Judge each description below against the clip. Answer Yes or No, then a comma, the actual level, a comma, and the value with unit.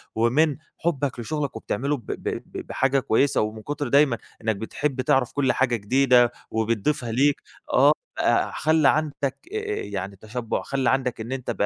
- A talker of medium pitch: No, low, 130 Hz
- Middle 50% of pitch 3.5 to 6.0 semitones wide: Yes, average, 3.8 semitones